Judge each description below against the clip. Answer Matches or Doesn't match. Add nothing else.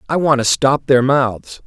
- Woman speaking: Doesn't match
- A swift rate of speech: Matches